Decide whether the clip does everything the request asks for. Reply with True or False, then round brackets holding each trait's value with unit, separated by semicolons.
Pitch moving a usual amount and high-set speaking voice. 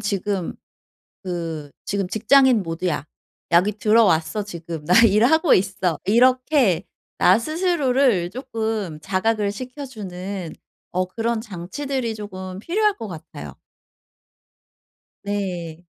True (4.7 semitones; 200 Hz)